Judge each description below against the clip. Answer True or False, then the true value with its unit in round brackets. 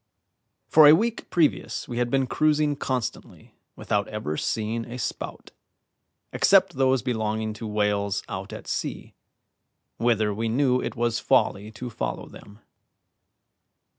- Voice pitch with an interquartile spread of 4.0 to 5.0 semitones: False (3.6 semitones)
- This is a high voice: False (115 Hz)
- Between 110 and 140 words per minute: True (135 wpm)